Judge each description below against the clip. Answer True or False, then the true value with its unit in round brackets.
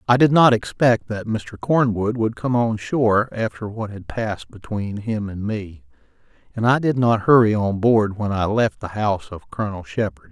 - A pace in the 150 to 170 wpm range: False (200 wpm)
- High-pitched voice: False (110 Hz)